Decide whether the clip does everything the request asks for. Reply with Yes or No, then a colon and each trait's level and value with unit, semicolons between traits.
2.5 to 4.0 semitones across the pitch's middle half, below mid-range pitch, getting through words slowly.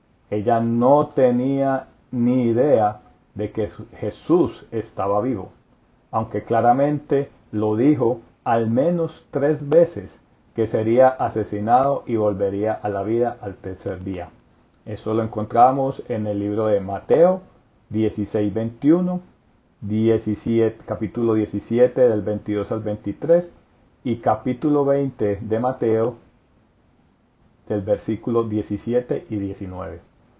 Yes: average, 3.2 semitones; low, 110 Hz; slow, 110 wpm